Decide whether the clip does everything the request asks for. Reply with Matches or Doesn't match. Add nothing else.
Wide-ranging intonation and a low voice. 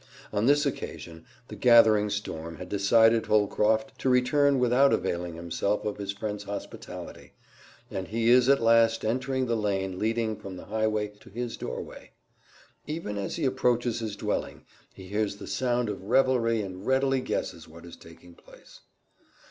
Doesn't match